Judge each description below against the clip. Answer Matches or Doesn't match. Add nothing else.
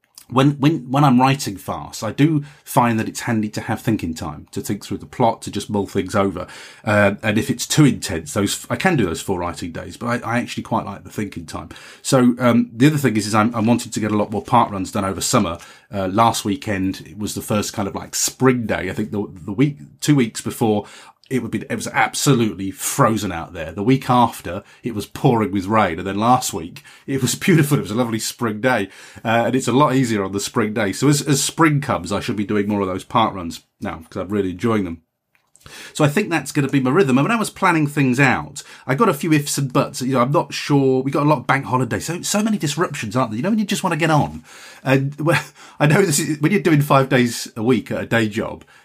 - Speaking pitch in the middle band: Doesn't match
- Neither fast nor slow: Doesn't match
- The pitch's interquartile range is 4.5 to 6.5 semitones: Matches